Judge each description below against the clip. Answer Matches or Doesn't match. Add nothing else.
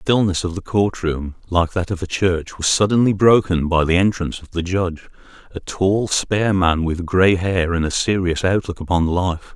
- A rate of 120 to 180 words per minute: Doesn't match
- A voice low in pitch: Matches